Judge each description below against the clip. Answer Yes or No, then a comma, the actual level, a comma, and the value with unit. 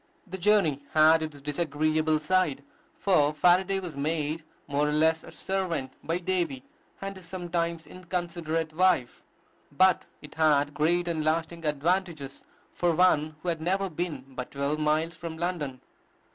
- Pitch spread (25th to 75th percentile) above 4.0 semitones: No, average, 2.8 semitones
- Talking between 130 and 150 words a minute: Yes, average, 145 wpm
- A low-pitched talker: No, medium, 160 Hz